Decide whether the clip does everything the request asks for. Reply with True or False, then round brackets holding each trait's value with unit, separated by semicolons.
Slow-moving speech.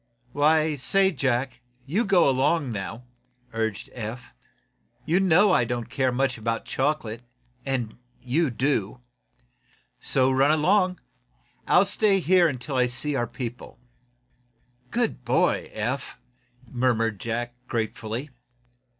True (120 wpm)